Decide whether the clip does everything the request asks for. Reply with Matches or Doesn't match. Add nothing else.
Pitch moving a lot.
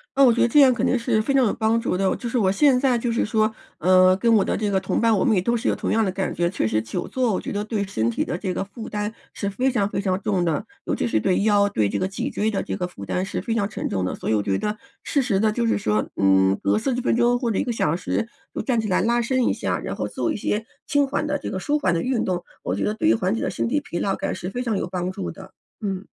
Doesn't match